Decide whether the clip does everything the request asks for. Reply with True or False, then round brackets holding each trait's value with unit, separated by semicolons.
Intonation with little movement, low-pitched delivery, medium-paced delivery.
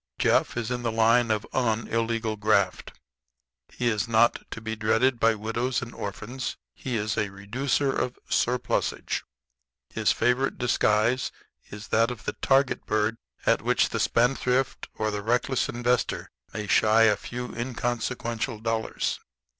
True (2.3 semitones; 115 Hz; 145 wpm)